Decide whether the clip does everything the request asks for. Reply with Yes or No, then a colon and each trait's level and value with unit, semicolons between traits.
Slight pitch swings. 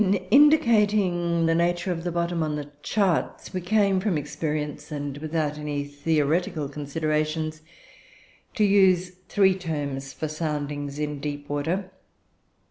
No: average, 3.8 semitones